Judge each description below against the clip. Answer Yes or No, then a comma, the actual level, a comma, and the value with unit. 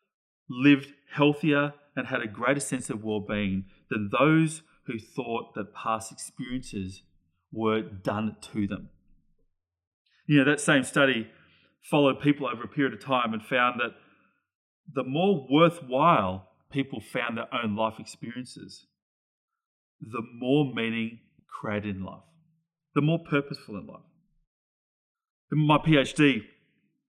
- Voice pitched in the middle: No, low, 130 Hz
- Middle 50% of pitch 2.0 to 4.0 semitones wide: No, average, 5.3 semitones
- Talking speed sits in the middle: No, slow, 130 wpm